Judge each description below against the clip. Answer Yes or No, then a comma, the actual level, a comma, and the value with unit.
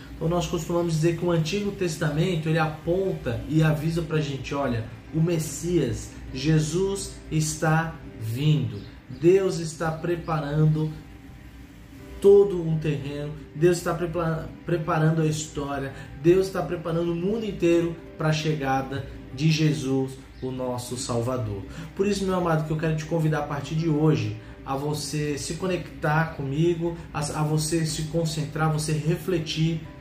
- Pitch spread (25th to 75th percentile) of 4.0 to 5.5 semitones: No, average, 3.2 semitones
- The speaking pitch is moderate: Yes, medium, 155 Hz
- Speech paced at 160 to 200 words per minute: No, average, 145 wpm